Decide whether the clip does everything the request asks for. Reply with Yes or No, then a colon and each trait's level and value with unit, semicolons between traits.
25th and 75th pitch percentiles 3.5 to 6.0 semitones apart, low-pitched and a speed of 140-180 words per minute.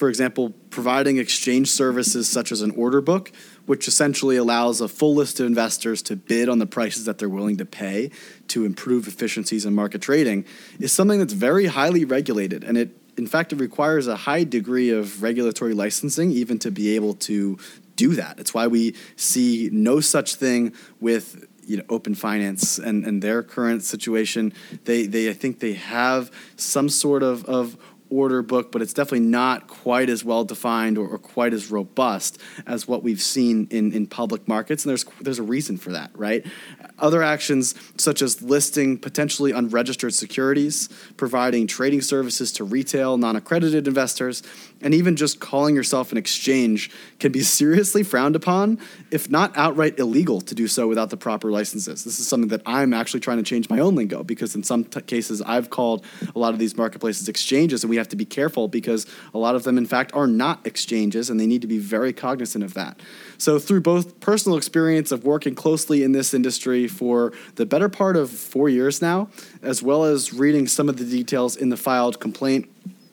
No: average, 4.0 semitones; low, 125 Hz; average, 195 wpm